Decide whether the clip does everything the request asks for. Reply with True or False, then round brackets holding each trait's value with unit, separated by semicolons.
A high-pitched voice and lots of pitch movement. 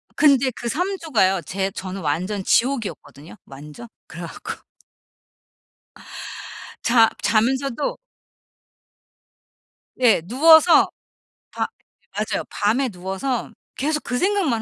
True (235 Hz; 6.4 semitones)